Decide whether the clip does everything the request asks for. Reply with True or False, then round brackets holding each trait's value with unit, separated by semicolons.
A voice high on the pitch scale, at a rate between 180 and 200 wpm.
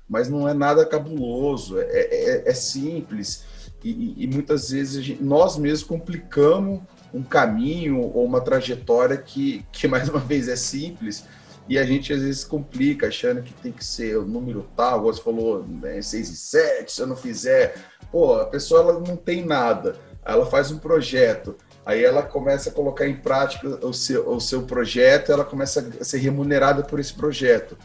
False (150 Hz; 185 wpm)